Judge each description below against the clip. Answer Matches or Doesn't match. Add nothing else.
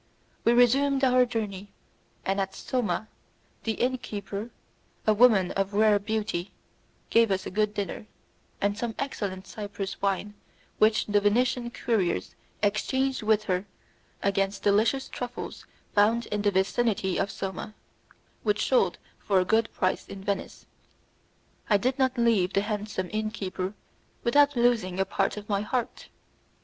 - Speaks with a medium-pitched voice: Doesn't match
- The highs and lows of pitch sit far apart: Doesn't match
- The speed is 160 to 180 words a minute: Doesn't match